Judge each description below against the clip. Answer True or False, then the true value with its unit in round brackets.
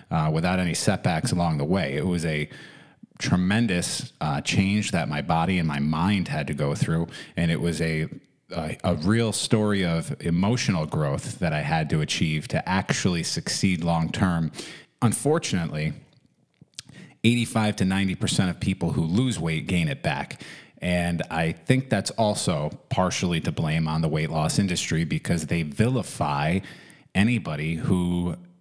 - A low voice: True (90 Hz)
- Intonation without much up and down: False (4.3 semitones)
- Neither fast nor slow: True (160 wpm)